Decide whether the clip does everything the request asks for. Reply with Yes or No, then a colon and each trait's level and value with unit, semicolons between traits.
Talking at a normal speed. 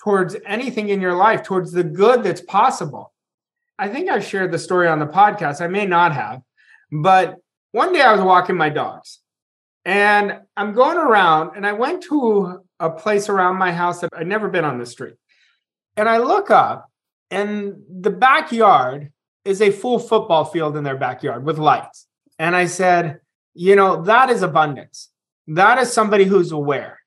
Yes: average, 180 wpm